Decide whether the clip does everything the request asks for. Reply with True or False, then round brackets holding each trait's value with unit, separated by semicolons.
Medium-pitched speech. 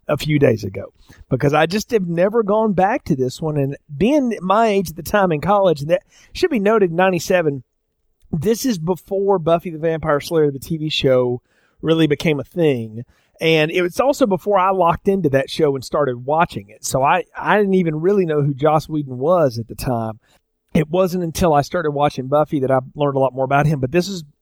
True (160 Hz)